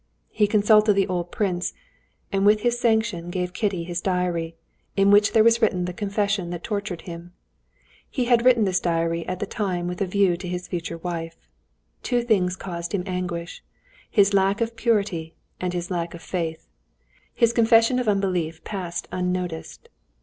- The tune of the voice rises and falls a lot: No, average, 3.2 semitones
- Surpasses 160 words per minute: Yes, average, 170 wpm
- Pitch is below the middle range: No, medium, 185 Hz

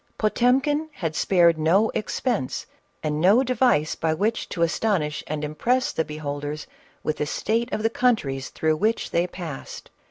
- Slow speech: No, average, 155 wpm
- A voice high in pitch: No, medium, 175 Hz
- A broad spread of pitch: Yes, wide, 7.0 semitones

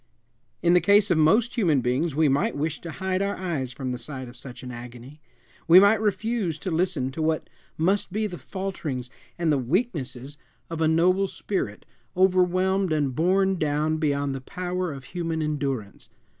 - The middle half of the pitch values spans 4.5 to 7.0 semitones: Yes, average, 5.2 semitones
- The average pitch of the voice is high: No, medium, 160 Hz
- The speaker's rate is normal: Yes, average, 180 wpm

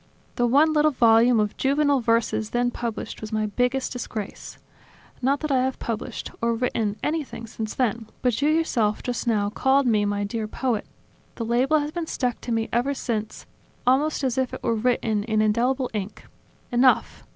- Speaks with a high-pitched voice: Yes, high, 240 Hz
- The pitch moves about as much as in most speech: Yes, average, 3.2 semitones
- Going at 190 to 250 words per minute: No, average, 180 wpm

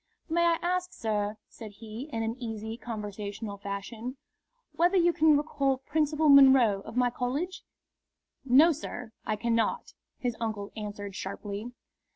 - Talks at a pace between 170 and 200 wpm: No, average, 140 wpm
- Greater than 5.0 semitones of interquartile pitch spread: Yes, wide, 5.4 semitones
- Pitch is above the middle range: Yes, high, 235 Hz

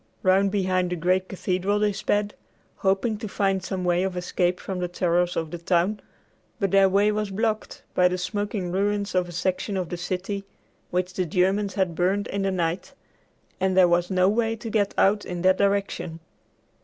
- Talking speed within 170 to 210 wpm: Yes, average, 190 wpm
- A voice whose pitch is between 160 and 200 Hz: Yes, high, 190 Hz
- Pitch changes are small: Yes, narrow, 2.0 semitones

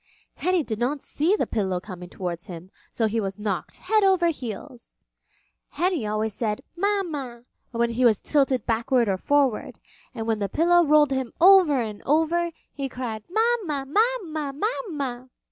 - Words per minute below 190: Yes, average, 160 wpm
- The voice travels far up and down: Yes, wide, 7.5 semitones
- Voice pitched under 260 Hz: No, very high, 265 Hz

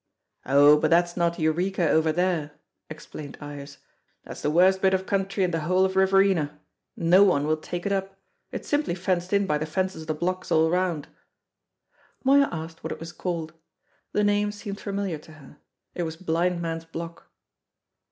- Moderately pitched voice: Yes, medium, 175 Hz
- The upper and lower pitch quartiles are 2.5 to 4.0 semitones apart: Yes, average, 3.2 semitones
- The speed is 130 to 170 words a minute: No, average, 180 wpm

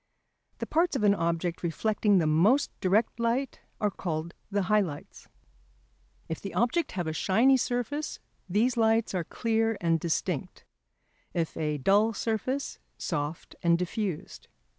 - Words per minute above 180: No, average, 140 wpm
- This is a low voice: No, high, 200 Hz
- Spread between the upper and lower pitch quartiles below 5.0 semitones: No, average, 5.3 semitones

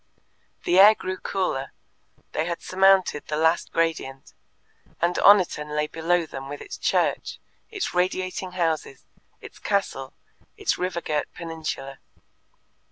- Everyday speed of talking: No, slow, 125 wpm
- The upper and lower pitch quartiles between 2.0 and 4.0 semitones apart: Yes, average, 3.5 semitones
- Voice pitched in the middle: Yes, medium, 170 Hz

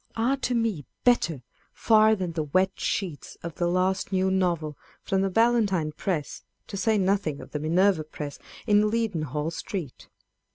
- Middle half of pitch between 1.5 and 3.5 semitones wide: No, average, 5.0 semitones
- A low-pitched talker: No, high, 190 Hz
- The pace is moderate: Yes, average, 160 wpm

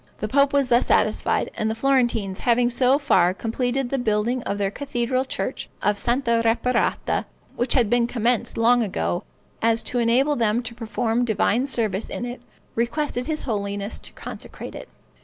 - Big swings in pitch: No, narrow, 2.4 semitones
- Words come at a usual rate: Yes, average, 170 wpm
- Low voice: No, high, 235 Hz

